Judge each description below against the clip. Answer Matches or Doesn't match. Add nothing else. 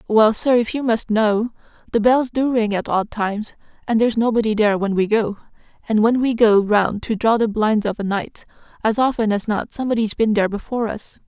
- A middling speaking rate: Doesn't match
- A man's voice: Doesn't match